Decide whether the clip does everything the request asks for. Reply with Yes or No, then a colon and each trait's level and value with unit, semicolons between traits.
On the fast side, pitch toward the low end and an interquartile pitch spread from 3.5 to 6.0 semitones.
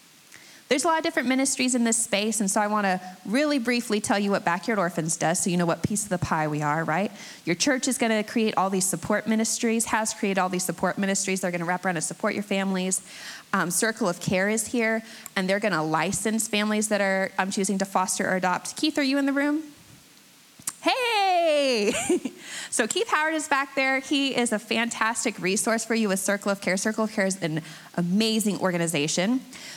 No: fast, 210 wpm; high, 210 Hz; average, 4.3 semitones